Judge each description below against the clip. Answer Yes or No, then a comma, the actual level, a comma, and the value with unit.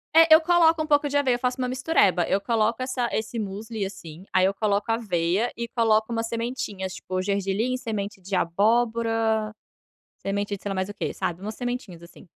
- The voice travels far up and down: No, average, 3.8 semitones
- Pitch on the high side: Yes, high, 220 Hz